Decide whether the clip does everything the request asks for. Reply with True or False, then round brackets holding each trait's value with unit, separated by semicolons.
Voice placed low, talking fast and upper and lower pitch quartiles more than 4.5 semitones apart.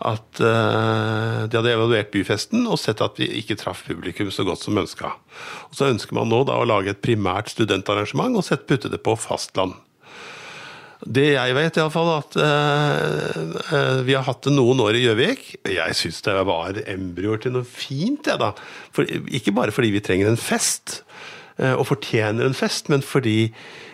False (120 Hz; 175 wpm; 5.3 semitones)